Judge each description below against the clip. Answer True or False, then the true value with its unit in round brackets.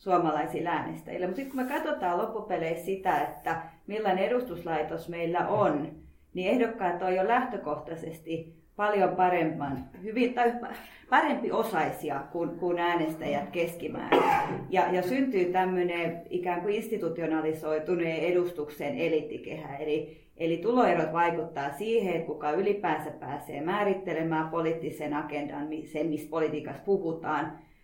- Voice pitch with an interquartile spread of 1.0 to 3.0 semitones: False (3.5 semitones)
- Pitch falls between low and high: True (170 Hz)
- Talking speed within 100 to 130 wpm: True (115 wpm)